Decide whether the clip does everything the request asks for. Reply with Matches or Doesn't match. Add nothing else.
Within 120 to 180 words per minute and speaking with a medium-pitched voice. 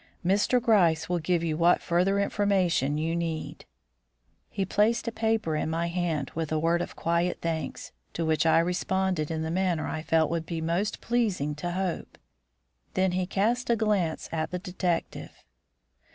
Matches